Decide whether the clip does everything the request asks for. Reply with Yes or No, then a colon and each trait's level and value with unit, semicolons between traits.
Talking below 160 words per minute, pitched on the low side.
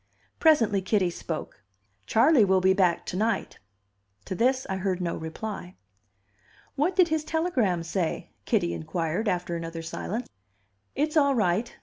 No: average, 140 wpm; high, 195 Hz